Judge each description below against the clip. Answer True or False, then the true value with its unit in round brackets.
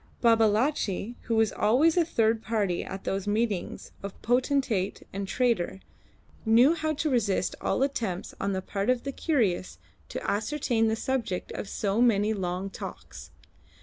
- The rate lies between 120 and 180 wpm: True (150 wpm)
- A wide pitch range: False (4.2 semitones)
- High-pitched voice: True (220 Hz)